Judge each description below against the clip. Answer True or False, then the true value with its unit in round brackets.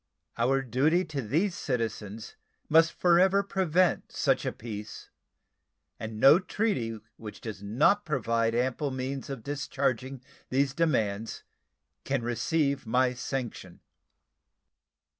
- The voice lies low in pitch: True (130 Hz)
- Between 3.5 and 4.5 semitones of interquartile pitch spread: False (5.4 semitones)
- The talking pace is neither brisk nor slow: False (110 wpm)